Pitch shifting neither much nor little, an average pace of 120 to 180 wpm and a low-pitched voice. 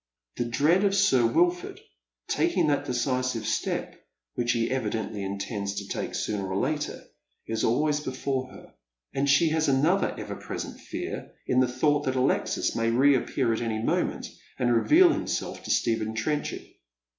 Yes: average, 4.4 semitones; average, 155 wpm; low, 130 Hz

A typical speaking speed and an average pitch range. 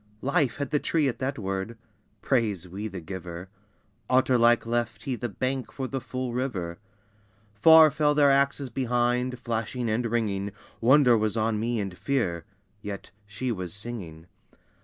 Yes: average, 160 wpm; average, 4.3 semitones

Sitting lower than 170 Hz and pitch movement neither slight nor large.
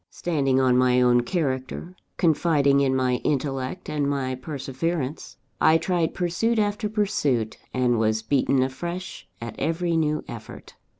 Yes: medium, 140 Hz; average, 4.9 semitones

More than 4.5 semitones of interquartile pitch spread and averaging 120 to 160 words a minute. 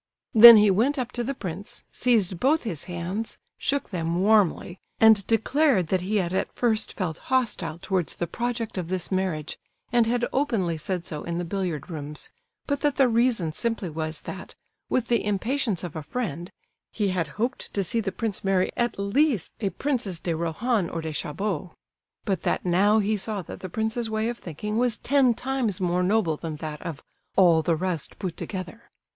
No: average, 5.3 semitones; average, 190 wpm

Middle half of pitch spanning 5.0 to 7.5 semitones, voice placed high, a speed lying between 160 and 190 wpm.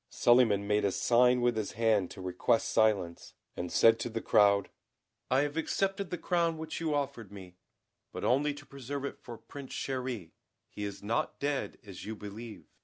No: wide, 5.4 semitones; low, 120 Hz; average, 180 wpm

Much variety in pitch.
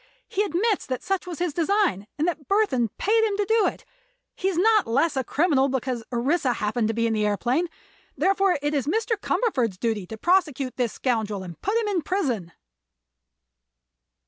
Yes: wide, 8.7 semitones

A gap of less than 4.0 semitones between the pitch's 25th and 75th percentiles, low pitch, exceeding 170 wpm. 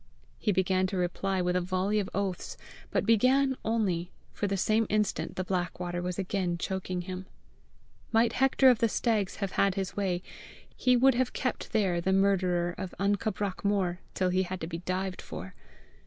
No: average, 2.7 semitones; high, 190 Hz; average, 185 wpm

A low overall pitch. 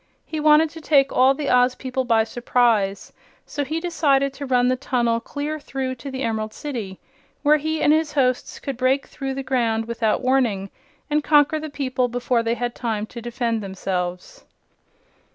No: very high, 255 Hz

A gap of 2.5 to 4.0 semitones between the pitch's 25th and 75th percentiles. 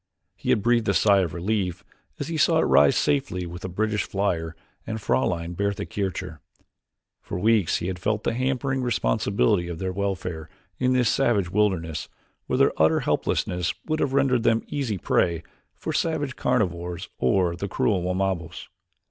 No: average, 5.1 semitones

